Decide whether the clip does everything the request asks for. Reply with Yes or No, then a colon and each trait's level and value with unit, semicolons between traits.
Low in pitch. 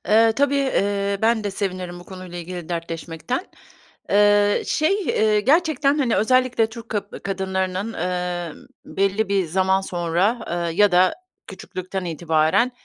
No: high, 195 Hz